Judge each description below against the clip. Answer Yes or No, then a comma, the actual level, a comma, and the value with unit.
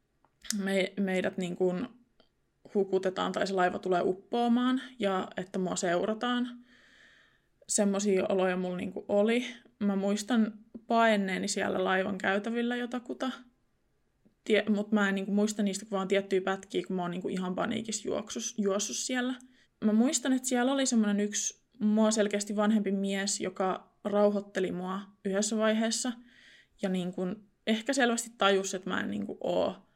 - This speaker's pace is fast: No, average, 145 wpm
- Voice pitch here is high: Yes, high, 205 Hz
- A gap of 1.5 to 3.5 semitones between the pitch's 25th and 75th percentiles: Yes, average, 3.2 semitones